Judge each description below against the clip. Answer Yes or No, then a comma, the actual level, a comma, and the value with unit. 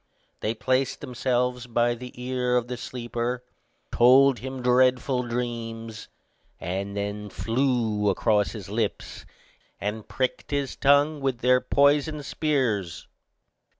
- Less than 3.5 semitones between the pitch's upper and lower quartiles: Yes, narrow, 2.5 semitones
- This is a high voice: No, low, 125 Hz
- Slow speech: Yes, slow, 115 wpm